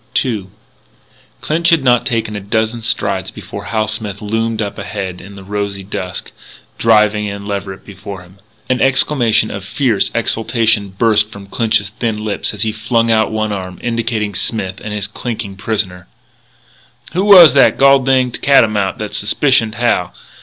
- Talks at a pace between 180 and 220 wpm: No, average, 160 wpm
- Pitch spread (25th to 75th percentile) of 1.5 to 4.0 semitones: Yes, narrow, 2.5 semitones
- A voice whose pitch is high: No, low, 110 Hz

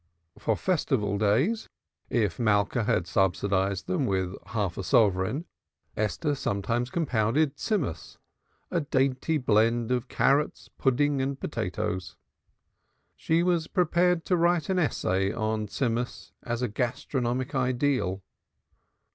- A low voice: Yes, low, 120 Hz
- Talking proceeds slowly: Yes, slow, 115 wpm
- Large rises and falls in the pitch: Yes, wide, 6.1 semitones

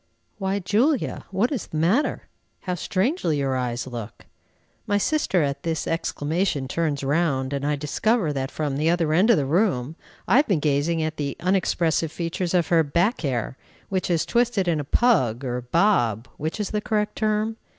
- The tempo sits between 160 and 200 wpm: Yes, average, 180 wpm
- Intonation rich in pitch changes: Yes, wide, 6.1 semitones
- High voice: No, medium, 165 Hz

